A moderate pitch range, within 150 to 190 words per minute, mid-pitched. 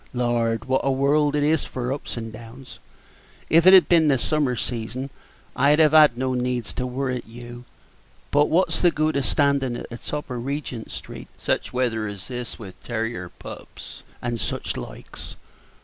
No: average, 3.5 semitones; average, 180 wpm; low, 125 Hz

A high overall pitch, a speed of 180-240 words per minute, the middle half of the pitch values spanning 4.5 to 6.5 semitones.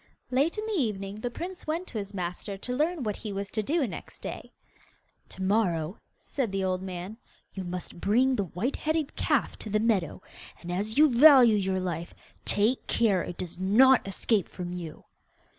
Yes: high, 210 Hz; average, 190 wpm; wide, 5.5 semitones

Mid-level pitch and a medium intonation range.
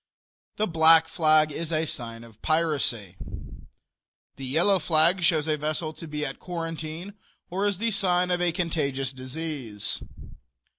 Yes: medium, 160 Hz; average, 3.3 semitones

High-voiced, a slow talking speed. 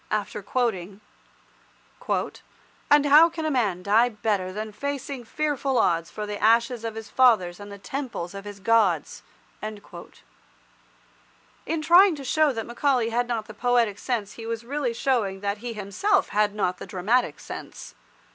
No: high, 225 Hz; average, 155 wpm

